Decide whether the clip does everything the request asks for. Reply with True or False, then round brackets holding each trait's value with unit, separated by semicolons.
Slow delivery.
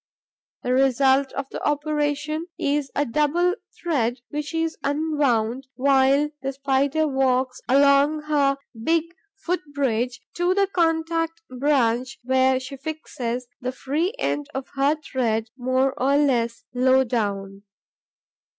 True (125 wpm)